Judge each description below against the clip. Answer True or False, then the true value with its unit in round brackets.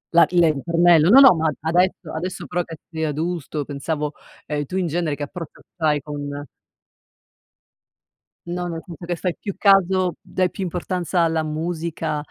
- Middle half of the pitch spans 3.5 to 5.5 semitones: False (2.6 semitones)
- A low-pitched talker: False (165 Hz)